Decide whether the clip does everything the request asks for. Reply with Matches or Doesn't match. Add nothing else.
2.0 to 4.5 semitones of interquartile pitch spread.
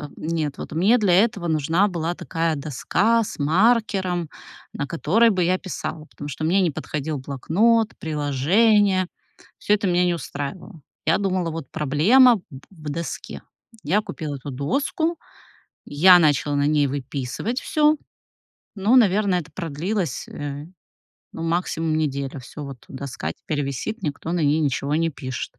Doesn't match